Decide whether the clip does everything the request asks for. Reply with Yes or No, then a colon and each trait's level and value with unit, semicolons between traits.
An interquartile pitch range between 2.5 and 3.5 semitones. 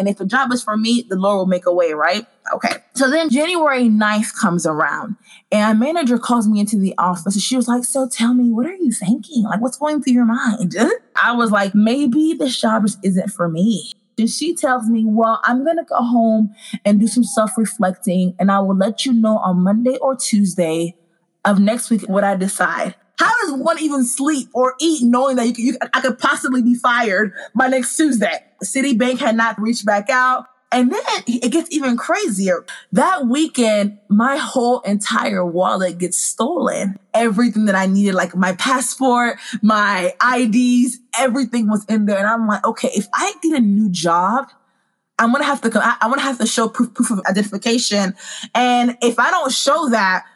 No: average, 3.9 semitones